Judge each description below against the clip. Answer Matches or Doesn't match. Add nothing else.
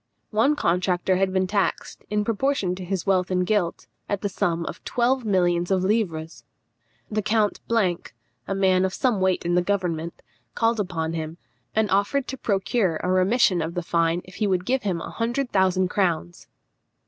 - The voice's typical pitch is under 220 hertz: Matches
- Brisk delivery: Doesn't match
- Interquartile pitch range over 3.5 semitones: Doesn't match